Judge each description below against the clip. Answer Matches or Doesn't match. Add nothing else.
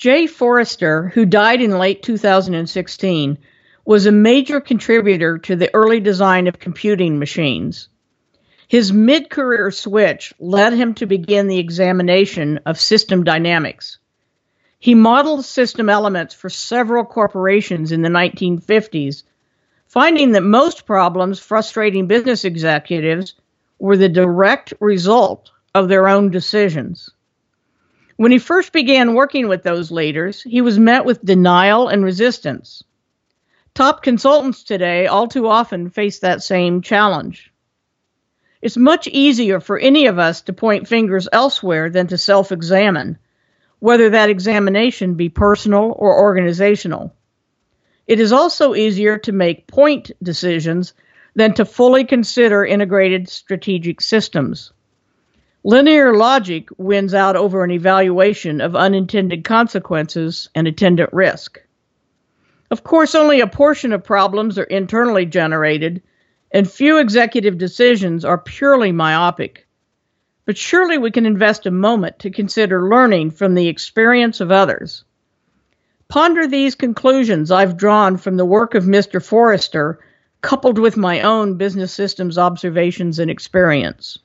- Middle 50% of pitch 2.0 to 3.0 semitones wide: Doesn't match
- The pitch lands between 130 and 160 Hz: Doesn't match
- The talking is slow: Matches